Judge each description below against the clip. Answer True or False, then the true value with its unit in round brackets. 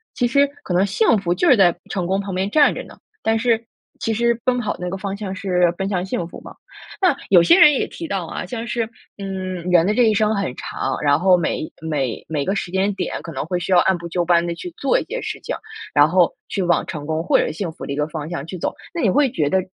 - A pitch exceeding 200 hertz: False (190 Hz)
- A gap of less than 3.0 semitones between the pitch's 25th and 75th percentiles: False (4.2 semitones)